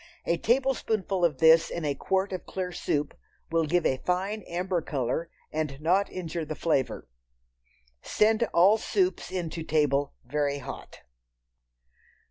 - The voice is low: No, medium, 170 Hz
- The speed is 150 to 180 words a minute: No, average, 140 wpm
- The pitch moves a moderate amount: Yes, average, 4.1 semitones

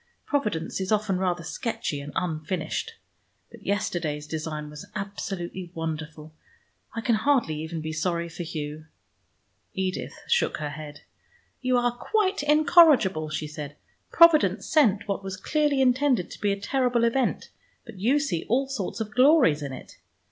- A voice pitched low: No, high, 195 Hz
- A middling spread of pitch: No, wide, 8.0 semitones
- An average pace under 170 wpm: Yes, average, 150 wpm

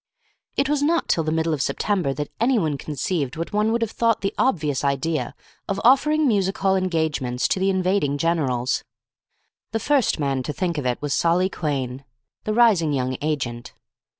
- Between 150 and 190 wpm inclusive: Yes, average, 180 wpm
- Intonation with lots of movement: Yes, wide, 6.5 semitones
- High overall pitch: No, medium, 165 Hz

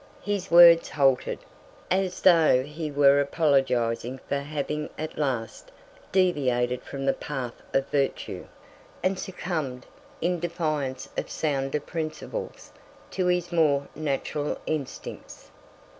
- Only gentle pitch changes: No, average, 3.8 semitones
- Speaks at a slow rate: Yes, slow, 115 wpm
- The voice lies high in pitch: No, medium, 150 Hz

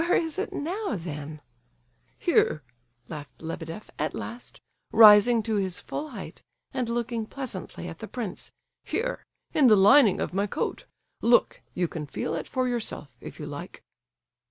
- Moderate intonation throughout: No, wide, 6.9 semitones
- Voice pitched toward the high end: Yes, high, 215 Hz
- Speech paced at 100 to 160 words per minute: Yes, average, 155 wpm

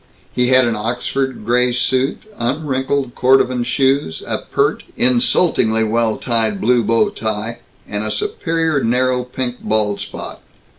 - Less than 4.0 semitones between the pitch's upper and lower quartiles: Yes, average, 2.7 semitones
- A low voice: Yes, low, 125 Hz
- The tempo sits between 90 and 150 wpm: Yes, slow, 135 wpm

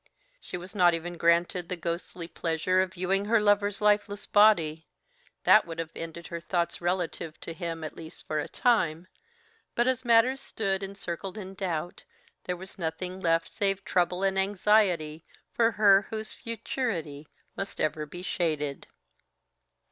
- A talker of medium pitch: Yes, medium, 180 Hz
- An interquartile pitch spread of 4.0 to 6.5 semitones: No, average, 3.6 semitones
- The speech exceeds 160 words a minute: No, average, 155 wpm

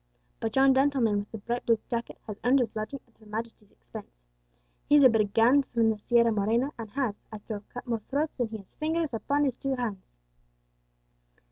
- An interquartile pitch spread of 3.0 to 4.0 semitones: Yes, average, 3.7 semitones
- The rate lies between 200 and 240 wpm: Yes, fast, 205 wpm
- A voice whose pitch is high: Yes, high, 230 Hz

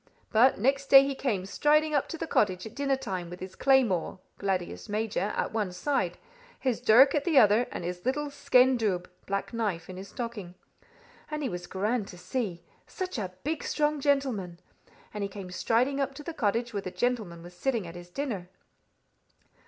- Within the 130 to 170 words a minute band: No, average, 195 wpm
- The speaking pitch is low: No, high, 225 Hz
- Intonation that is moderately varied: No, wide, 6.5 semitones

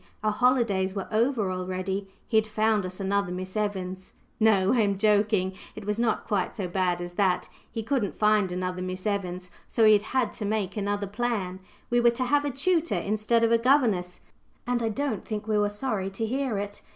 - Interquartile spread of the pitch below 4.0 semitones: Yes, average, 3.4 semitones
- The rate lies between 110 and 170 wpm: No, fast, 205 wpm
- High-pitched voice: Yes, high, 210 Hz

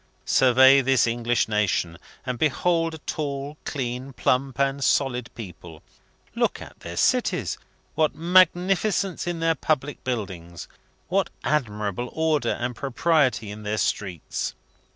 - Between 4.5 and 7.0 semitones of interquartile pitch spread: Yes, average, 5.2 semitones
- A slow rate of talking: Yes, slow, 125 wpm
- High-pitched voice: No, low, 130 Hz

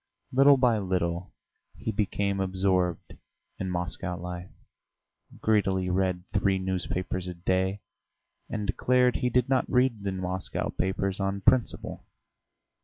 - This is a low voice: Yes, very low, 95 Hz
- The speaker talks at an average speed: No, slow, 120 wpm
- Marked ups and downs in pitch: No, narrow, 2.5 semitones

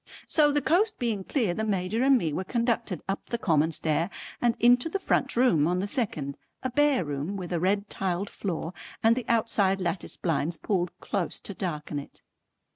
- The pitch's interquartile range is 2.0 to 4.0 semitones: No, wide, 5.6 semitones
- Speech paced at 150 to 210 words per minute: Yes, average, 195 wpm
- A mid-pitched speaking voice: No, high, 195 Hz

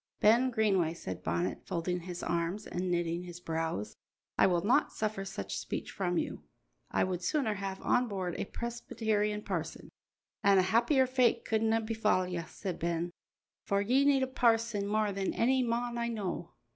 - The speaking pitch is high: Yes, high, 200 Hz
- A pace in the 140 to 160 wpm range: No, average, 170 wpm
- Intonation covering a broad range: No, average, 4.6 semitones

